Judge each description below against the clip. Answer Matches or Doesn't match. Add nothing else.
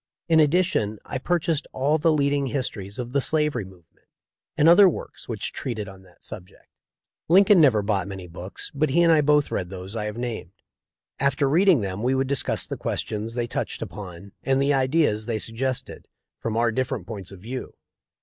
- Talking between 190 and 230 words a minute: Matches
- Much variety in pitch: Matches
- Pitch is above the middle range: Doesn't match